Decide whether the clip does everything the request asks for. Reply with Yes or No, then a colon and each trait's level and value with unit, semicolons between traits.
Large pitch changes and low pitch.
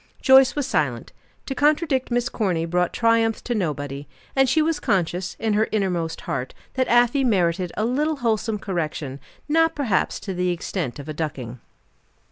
No: wide, 7.5 semitones; high, 210 Hz